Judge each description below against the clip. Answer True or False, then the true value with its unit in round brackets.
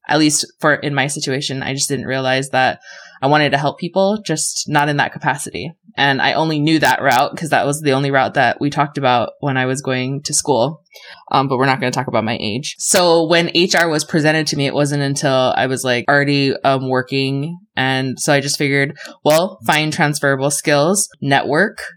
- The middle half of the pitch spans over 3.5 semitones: False (2.5 semitones)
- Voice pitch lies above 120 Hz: True (140 Hz)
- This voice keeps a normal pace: False (215 wpm)